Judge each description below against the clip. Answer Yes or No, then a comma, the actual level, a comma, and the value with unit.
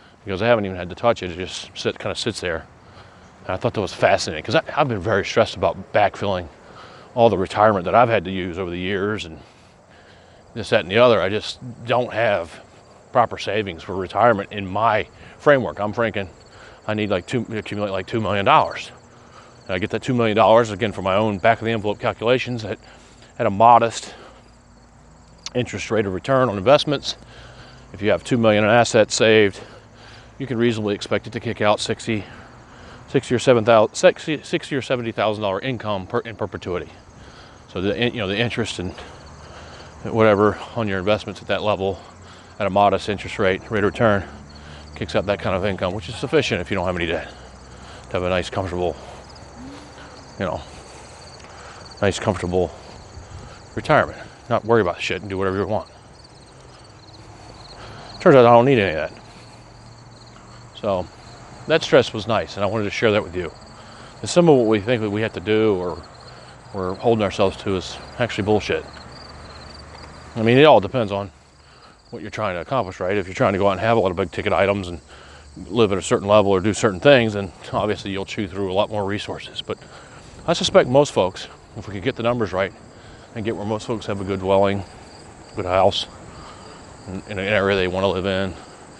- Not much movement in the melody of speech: No, average, 3.4 semitones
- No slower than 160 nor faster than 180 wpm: No, average, 200 wpm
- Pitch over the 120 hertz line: No, low, 105 Hz